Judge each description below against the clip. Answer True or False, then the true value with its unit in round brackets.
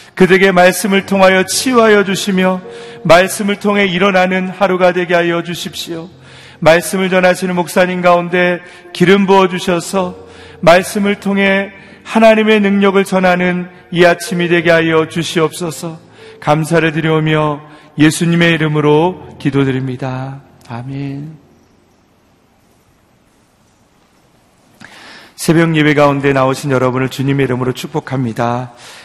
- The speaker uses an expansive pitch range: False (3.9 semitones)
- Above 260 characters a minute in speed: True (275 characters per minute)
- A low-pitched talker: False (175 Hz)